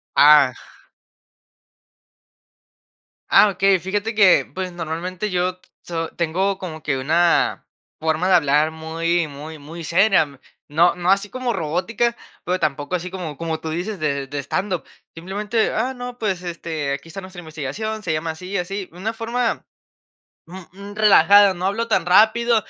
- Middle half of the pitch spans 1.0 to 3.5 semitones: No, average, 4.0 semitones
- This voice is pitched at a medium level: Yes, medium, 180 Hz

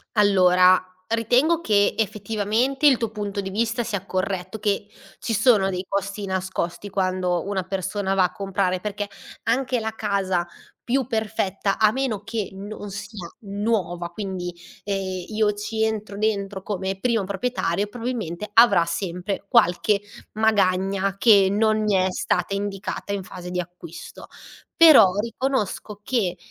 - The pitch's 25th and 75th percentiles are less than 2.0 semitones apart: No, average, 2.7 semitones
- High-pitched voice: Yes, high, 200 Hz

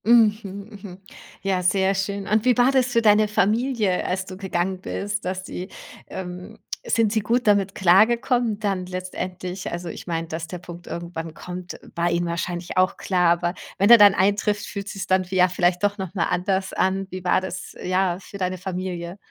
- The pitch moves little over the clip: Yes, narrow, 2.3 semitones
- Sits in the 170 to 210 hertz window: Yes, high, 190 Hz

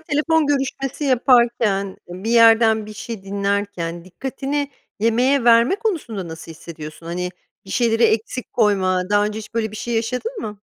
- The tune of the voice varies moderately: Yes, average, 4.3 semitones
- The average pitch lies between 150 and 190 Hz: No, high, 225 Hz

